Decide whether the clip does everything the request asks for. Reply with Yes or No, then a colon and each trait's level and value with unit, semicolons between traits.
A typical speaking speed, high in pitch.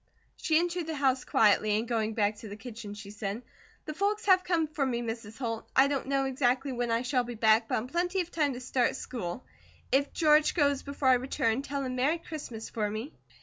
No: fast, 225 wpm; very high, 255 Hz